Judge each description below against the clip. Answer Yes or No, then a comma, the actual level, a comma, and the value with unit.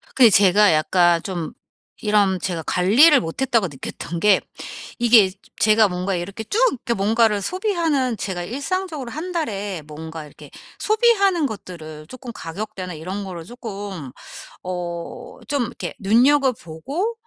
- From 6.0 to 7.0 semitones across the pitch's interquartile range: Yes, wide, 6.6 semitones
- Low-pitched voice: No, high, 205 Hz